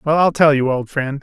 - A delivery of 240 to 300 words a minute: Yes, fast, 295 wpm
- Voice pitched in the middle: Yes, medium, 145 Hz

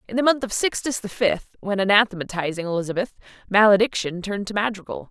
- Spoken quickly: No, average, 165 wpm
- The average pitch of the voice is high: Yes, high, 205 Hz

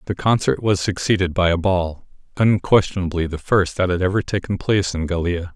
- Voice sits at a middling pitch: No, very low, 95 Hz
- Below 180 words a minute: No, average, 185 wpm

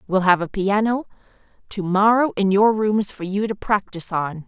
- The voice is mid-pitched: No, high, 200 Hz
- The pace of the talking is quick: No, average, 175 wpm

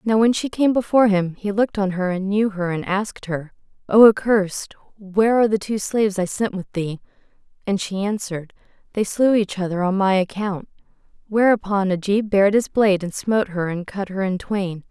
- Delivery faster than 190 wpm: Yes, average, 200 wpm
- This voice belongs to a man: No, female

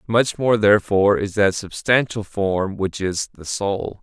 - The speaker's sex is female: No, male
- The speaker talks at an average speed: Yes, average, 165 wpm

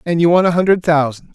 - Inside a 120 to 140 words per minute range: No, fast, 265 wpm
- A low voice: No, medium, 165 Hz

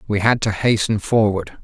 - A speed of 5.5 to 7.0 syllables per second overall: No, 4.9 syllables/s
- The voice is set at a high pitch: No, low, 105 Hz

